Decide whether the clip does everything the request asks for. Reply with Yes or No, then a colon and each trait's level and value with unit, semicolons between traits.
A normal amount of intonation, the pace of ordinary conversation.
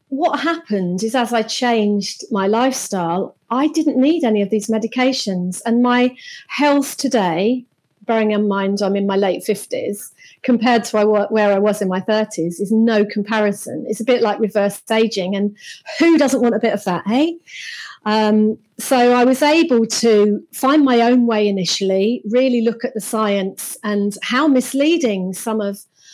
Yes: average, 3.9 semitones; average, 170 wpm